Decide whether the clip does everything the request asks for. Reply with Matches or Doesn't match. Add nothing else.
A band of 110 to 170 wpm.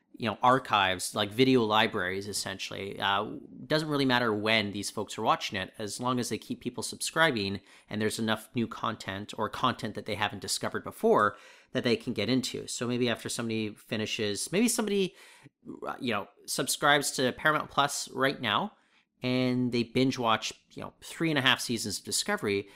Doesn't match